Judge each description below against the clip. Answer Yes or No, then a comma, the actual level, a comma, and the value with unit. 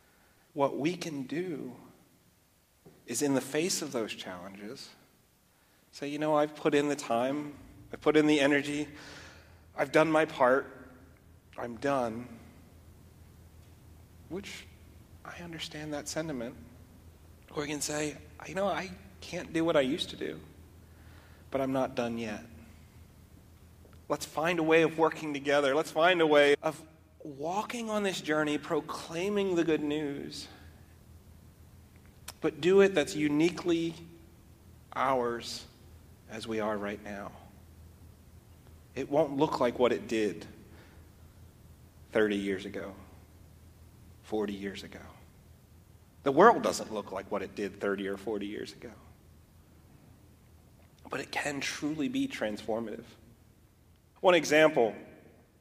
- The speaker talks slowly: Yes, slow, 130 wpm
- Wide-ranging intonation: Yes, wide, 8.9 semitones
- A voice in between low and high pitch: No, low, 110 Hz